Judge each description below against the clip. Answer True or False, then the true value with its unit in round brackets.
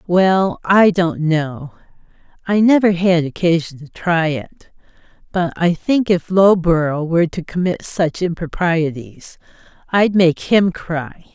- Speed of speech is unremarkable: False (130 wpm)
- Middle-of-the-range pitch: True (170 Hz)